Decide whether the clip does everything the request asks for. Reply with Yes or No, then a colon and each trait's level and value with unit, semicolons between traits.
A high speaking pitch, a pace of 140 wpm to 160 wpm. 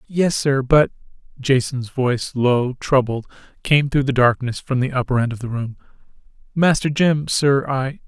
No: low, 130 Hz; average, 150 wpm